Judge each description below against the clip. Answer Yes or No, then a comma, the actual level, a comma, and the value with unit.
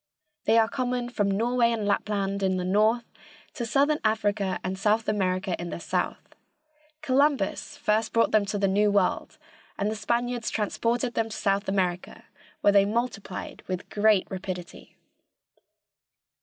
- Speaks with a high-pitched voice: Yes, high, 210 Hz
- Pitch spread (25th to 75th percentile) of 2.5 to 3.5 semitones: Yes, average, 2.9 semitones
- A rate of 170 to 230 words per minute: No, average, 150 wpm